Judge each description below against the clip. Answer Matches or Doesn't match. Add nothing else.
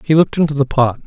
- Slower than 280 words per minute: Doesn't match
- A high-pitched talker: Doesn't match